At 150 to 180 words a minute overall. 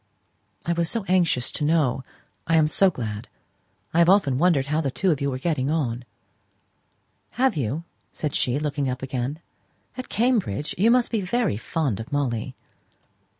Yes: average, 160 wpm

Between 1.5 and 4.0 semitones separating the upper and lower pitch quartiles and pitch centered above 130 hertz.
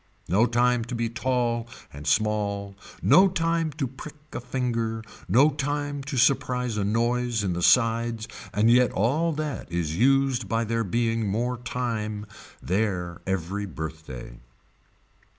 No: average, 3.6 semitones; low, 115 Hz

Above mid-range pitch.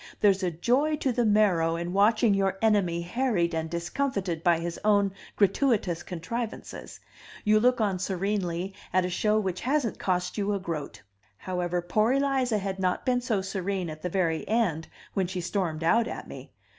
Yes: high, 195 Hz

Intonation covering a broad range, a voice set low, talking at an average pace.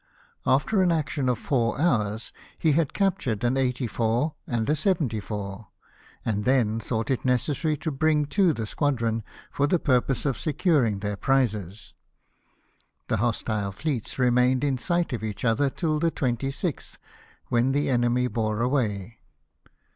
No: average, 4.7 semitones; low, 125 Hz; average, 145 wpm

